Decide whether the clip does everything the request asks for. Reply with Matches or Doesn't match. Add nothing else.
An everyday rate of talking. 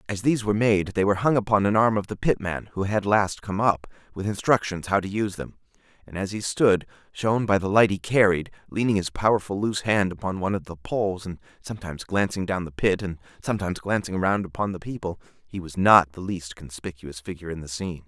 Doesn't match